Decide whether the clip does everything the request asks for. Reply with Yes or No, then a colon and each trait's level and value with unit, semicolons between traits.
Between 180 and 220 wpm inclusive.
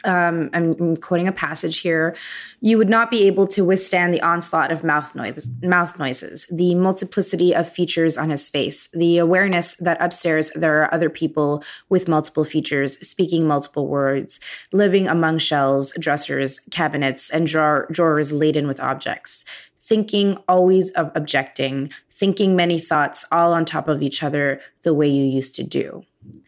No: average, 165 wpm